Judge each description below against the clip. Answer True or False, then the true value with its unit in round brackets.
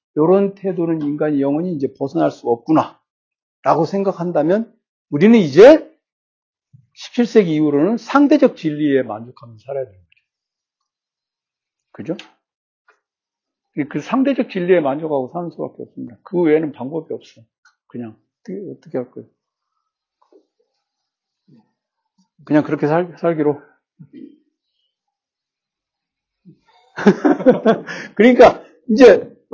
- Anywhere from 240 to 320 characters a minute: False (230 characters per minute)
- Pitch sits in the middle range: True (175 Hz)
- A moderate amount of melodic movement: False (9.0 semitones)